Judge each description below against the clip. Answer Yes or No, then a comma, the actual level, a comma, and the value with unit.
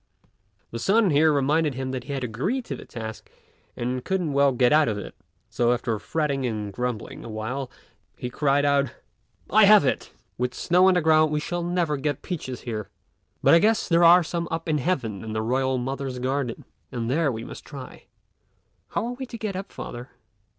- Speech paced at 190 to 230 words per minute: Yes, average, 200 wpm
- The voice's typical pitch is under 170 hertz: Yes, medium, 140 Hz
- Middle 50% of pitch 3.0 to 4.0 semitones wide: No, average, 5.3 semitones